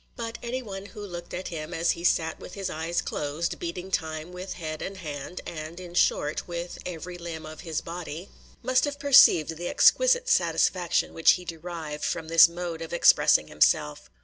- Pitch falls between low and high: Yes, medium, 170 Hz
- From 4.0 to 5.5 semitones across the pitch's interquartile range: No, narrow, 2.5 semitones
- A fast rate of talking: No, average, 185 wpm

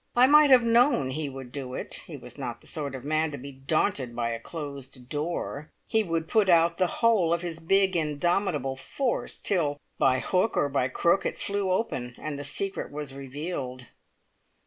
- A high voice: No, medium, 155 Hz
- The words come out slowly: No, average, 190 wpm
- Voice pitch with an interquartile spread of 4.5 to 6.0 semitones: Yes, wide, 5.6 semitones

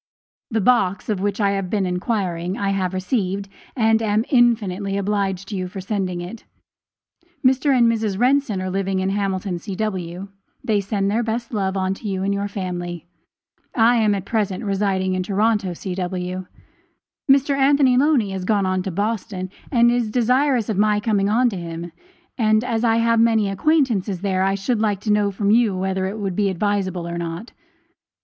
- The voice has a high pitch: Yes, high, 200 Hz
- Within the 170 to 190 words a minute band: Yes, average, 180 wpm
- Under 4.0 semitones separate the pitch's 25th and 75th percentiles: Yes, average, 3.1 semitones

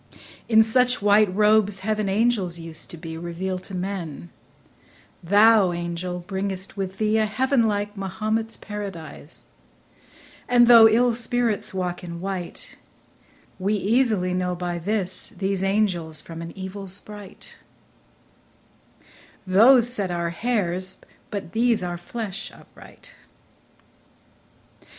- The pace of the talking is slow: Yes, slow, 120 wpm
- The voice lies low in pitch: No, high, 195 Hz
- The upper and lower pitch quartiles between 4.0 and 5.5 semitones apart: No, average, 3.4 semitones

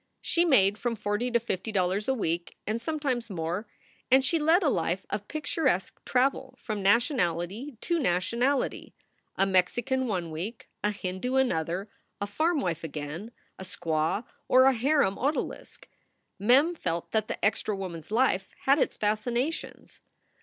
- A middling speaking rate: Yes, average, 155 wpm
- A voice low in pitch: No, high, 215 Hz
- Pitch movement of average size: No, wide, 6.1 semitones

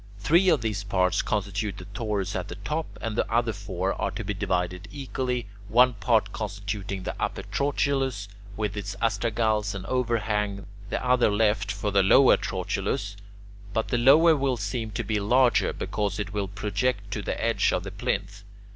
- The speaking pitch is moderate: No, low, 105 Hz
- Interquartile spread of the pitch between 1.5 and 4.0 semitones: Yes, average, 3.2 semitones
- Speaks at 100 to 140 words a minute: No, average, 175 wpm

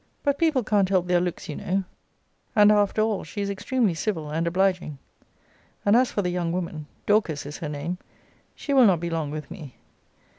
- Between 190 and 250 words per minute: Yes, average, 195 wpm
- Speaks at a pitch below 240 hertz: Yes, medium, 185 Hz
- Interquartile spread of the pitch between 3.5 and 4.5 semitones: Yes, average, 4.1 semitones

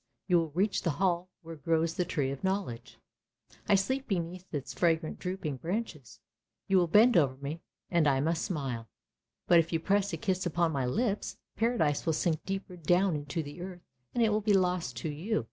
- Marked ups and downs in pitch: No, average, 4.2 semitones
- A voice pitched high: No, medium, 170 Hz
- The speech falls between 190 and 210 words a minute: Yes, average, 195 wpm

